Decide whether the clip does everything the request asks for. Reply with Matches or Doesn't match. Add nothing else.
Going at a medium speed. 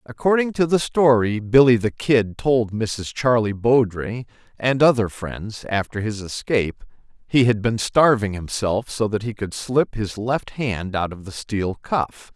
Matches